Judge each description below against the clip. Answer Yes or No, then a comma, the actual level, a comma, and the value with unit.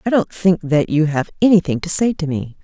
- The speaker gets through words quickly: Yes, fast, 250 wpm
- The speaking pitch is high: No, medium, 170 Hz